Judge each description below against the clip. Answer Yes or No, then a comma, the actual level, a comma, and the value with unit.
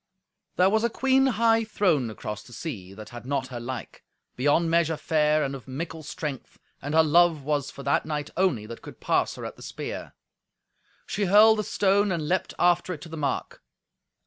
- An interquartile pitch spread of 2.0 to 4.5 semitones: No, wide, 5.4 semitones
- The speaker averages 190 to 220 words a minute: Yes, average, 200 wpm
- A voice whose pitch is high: No, medium, 155 Hz